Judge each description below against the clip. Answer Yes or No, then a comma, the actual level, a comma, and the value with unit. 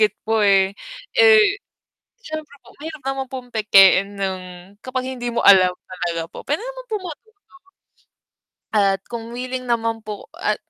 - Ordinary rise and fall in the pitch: No, wide, 7.3 semitones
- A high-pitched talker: Yes, high, 240 Hz